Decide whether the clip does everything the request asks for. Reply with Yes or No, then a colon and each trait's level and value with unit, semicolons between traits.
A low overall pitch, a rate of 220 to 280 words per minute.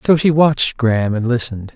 No: low, 125 Hz; fast, 205 wpm